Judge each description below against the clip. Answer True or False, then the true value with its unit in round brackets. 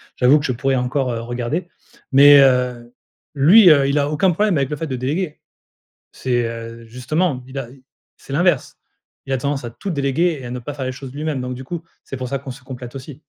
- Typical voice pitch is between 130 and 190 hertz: True (135 Hz)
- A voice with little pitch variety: False (3.0 semitones)